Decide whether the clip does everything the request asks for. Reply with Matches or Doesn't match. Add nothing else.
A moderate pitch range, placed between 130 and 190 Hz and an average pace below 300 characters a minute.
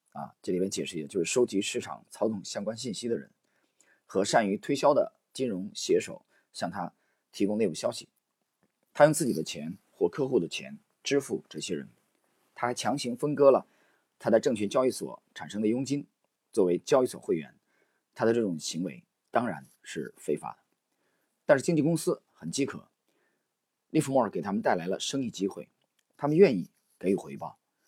Matches